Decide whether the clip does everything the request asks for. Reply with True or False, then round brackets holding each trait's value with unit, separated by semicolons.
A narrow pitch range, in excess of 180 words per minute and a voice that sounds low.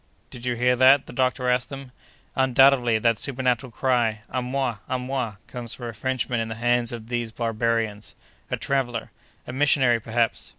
False (2.0 semitones; 175 wpm; 125 Hz)